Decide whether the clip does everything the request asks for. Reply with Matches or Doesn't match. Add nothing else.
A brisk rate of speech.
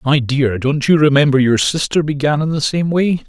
Matches